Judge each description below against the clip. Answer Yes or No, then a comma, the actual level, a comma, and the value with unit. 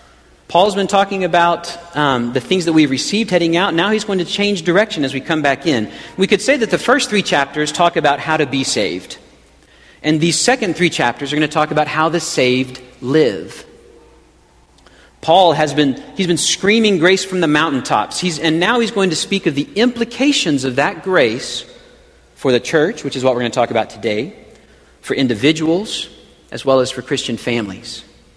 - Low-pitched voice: No, medium, 160 Hz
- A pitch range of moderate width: No, wide, 5.8 semitones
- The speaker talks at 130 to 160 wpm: No, average, 200 wpm